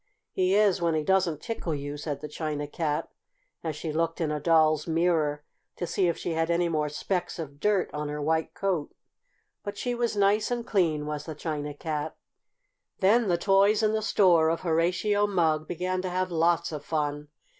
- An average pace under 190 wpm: No, average, 195 wpm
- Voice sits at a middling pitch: Yes, medium, 165 Hz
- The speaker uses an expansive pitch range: No, average, 3.7 semitones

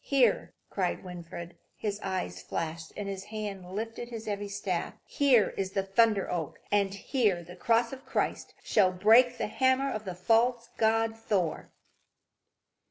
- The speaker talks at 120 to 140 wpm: No, average, 160 wpm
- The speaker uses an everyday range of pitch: Yes, average, 3.7 semitones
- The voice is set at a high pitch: Yes, high, 205 Hz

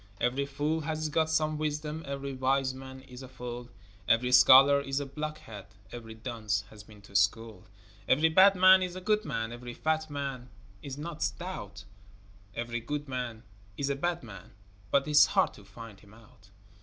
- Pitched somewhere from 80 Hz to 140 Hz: Yes, low, 135 Hz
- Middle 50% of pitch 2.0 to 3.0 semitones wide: No, average, 4.7 semitones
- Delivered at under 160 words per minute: No, average, 180 wpm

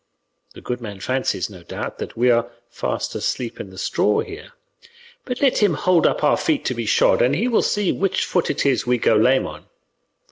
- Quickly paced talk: Yes, fast, 215 wpm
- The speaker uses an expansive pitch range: Yes, wide, 8.0 semitones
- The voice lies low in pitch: Yes, low, 130 Hz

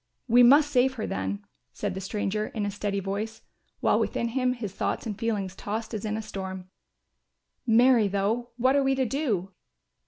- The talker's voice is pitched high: Yes, high, 215 Hz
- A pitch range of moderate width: Yes, average, 3.8 semitones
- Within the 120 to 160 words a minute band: No, average, 185 wpm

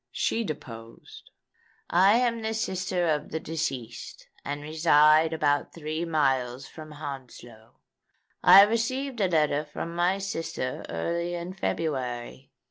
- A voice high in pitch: No, medium, 155 Hz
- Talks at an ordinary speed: No, slow, 125 wpm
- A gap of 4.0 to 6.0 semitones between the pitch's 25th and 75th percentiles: Yes, average, 4.5 semitones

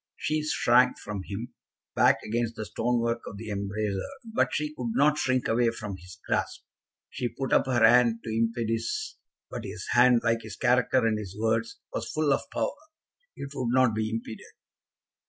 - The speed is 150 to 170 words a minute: No, average, 180 wpm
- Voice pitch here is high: No, low, 115 Hz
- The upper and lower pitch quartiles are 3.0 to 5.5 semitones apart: No, narrow, 2.6 semitones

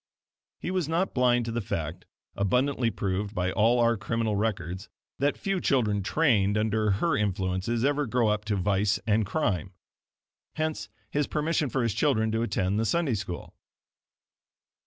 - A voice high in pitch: No, low, 110 Hz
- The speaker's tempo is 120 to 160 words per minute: Yes, average, 155 wpm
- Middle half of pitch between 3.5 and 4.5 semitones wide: No, average, 5.0 semitones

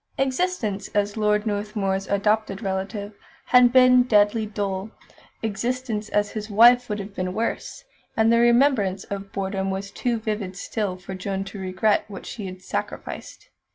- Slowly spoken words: No, average, 155 wpm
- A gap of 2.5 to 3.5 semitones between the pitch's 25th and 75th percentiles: Yes, average, 2.8 semitones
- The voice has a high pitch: Yes, high, 210 Hz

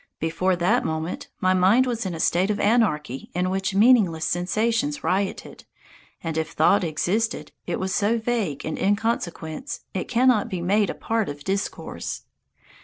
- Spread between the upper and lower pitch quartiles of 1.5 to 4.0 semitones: No, average, 4.6 semitones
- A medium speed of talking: Yes, average, 160 wpm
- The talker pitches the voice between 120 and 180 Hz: No, high, 190 Hz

